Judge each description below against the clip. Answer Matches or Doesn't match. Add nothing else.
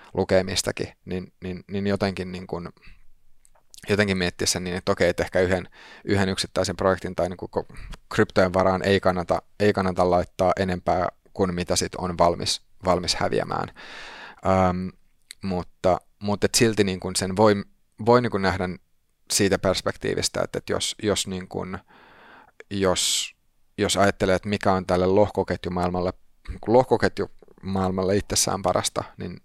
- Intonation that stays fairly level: Matches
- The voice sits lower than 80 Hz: Doesn't match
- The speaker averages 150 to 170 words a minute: Doesn't match